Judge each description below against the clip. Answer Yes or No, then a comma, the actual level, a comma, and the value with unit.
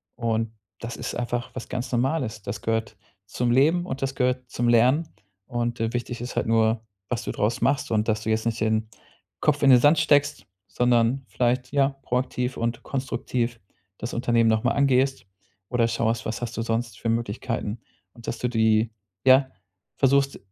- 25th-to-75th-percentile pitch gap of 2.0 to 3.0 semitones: Yes, narrow, 2.4 semitones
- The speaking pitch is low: Yes, low, 120 Hz